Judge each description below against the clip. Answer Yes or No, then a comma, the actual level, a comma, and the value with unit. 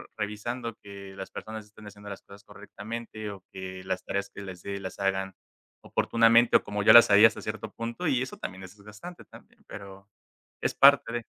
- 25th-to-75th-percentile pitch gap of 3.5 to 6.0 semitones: No, average, 2.8 semitones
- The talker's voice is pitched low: Yes, low, 105 Hz